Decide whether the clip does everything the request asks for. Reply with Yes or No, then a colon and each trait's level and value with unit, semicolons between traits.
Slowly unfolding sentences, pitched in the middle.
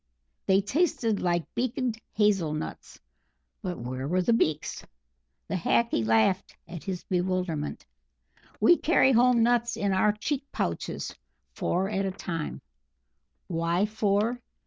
No: slow, 125 wpm; high, 195 Hz